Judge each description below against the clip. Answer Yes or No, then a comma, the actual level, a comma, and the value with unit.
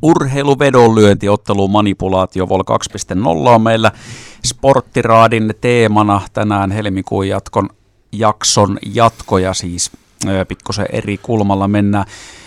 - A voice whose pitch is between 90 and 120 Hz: Yes, low, 105 Hz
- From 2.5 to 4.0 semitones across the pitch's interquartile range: Yes, average, 2.9 semitones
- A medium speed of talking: No, slow, 85 wpm